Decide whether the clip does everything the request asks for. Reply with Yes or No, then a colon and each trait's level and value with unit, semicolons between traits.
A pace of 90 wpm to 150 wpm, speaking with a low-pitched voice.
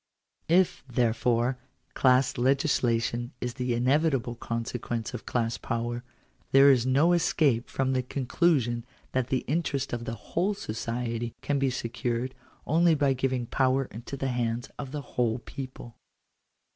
Yes: average, 140 wpm; low, 125 Hz